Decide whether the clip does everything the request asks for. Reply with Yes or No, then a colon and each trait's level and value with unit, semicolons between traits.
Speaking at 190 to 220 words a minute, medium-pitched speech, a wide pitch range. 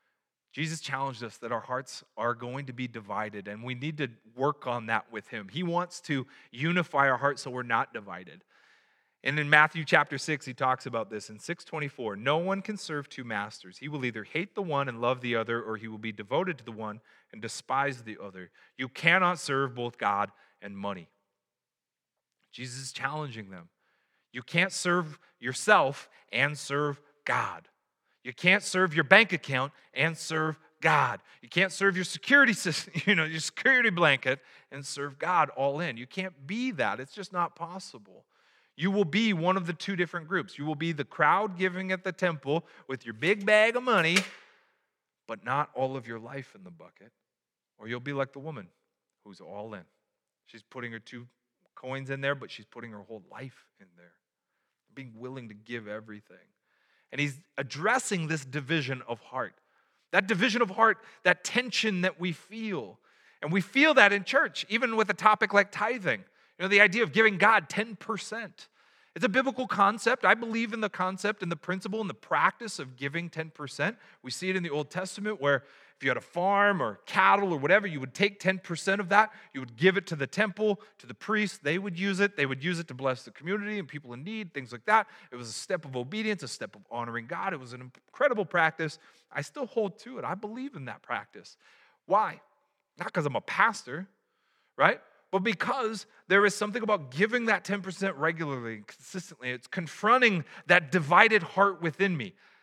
Yes: average, 200 wpm; medium, 160 Hz; wide, 7.3 semitones